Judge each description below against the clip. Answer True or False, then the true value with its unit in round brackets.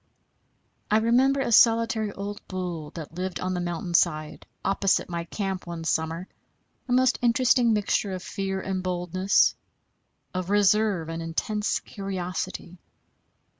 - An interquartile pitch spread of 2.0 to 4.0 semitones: True (3.5 semitones)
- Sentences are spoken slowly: True (130 wpm)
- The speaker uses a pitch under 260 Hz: True (190 Hz)